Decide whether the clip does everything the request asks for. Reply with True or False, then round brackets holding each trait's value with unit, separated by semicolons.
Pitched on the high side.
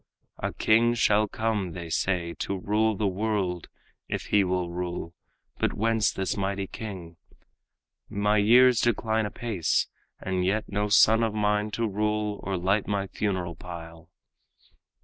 False (100 Hz)